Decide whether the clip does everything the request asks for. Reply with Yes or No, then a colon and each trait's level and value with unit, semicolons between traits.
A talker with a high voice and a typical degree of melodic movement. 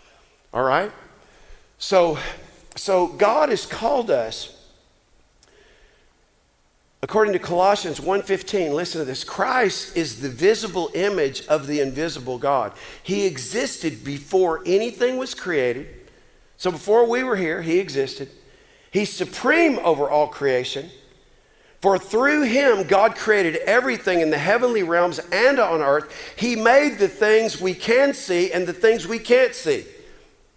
No: high, 195 Hz; wide, 6.7 semitones